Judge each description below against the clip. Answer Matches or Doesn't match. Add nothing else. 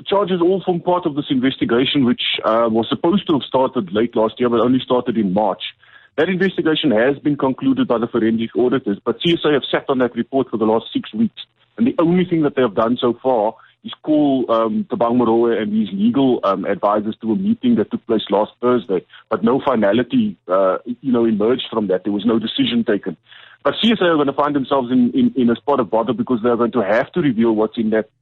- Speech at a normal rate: Doesn't match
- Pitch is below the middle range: Matches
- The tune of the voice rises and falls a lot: Matches